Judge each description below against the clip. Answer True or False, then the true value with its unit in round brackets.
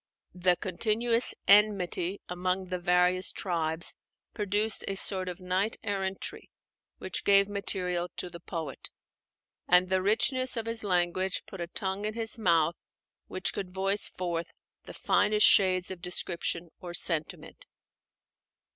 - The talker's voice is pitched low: False (185 Hz)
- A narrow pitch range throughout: True (2.3 semitones)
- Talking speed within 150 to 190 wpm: False (135 wpm)